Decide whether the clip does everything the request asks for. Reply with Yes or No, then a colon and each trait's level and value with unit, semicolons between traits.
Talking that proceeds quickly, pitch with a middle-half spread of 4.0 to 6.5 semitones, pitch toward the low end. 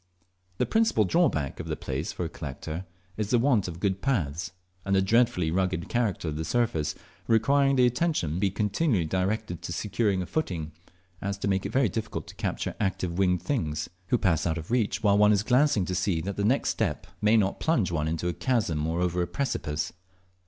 Yes: fast, 210 wpm; average, 5.2 semitones; very low, 95 Hz